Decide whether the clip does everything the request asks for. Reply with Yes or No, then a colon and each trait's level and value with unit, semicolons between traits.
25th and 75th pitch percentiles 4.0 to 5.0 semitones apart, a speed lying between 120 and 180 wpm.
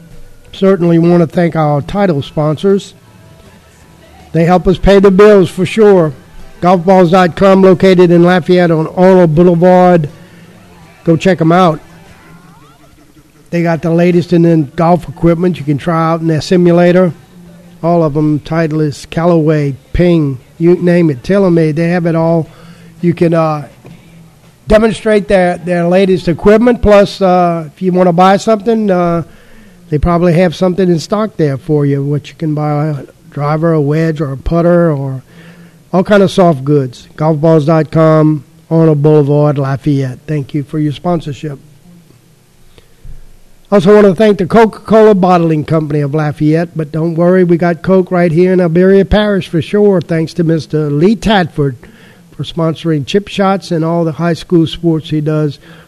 No: average, 2.8 semitones; average, 160 wpm